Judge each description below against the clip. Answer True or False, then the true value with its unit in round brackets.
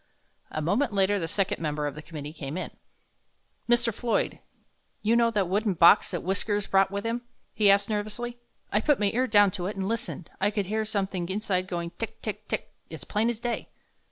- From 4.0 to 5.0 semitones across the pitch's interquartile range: False (3.2 semitones)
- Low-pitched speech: False (200 Hz)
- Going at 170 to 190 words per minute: False (205 wpm)